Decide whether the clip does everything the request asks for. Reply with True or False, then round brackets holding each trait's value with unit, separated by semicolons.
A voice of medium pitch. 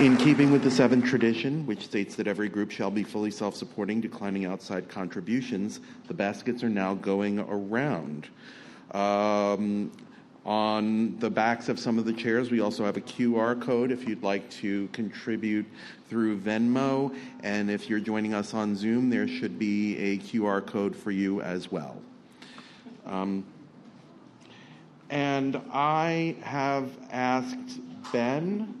False (110 Hz)